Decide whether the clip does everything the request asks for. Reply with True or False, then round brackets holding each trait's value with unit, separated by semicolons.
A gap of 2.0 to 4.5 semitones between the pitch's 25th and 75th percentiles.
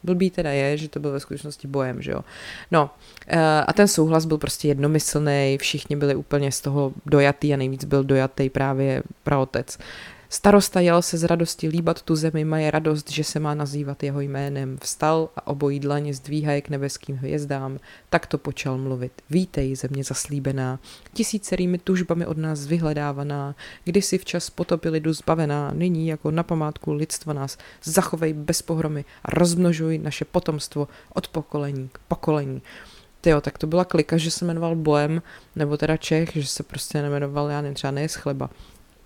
True (2.5 semitones)